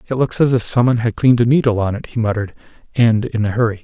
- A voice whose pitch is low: Yes, low, 115 Hz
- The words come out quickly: Yes, fast, 280 wpm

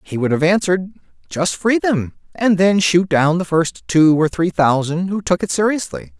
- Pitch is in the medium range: Yes, medium, 170 Hz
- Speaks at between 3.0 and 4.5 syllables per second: No, 4.8 syllables/s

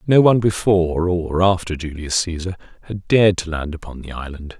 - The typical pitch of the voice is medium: No, very low, 90 Hz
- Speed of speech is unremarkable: Yes, average, 185 wpm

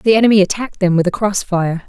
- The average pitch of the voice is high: Yes, high, 195 Hz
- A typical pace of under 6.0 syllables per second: No, 6.6 syllables/s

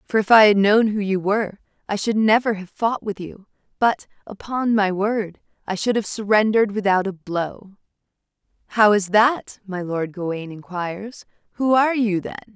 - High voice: Yes, high, 205 Hz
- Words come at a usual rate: Yes, average, 175 wpm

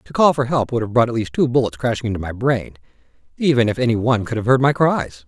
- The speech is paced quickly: Yes, fast, 275 wpm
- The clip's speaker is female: No, male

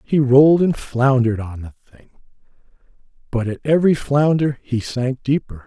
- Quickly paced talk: No, average, 150 wpm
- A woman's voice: No, male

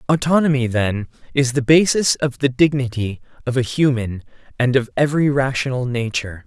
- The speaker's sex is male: Yes, male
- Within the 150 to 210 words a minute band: No, average, 140 wpm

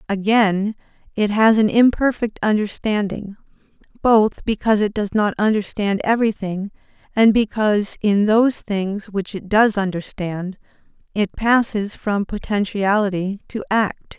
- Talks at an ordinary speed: No, slow, 120 wpm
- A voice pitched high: Yes, high, 205 Hz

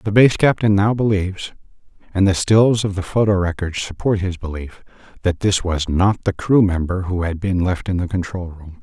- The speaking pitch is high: No, very low, 95 Hz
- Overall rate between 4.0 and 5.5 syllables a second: Yes, 5.0 syllables/s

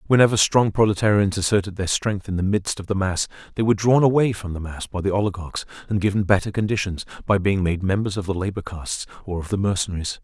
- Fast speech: Yes, fast, 225 wpm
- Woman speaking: No, male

